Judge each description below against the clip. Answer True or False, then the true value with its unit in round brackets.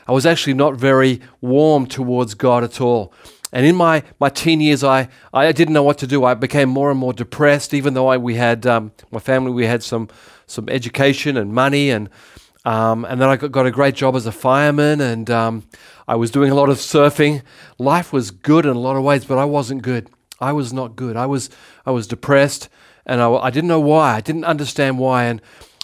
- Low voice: True (130 Hz)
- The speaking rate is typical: False (230 wpm)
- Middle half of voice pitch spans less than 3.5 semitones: True (2.8 semitones)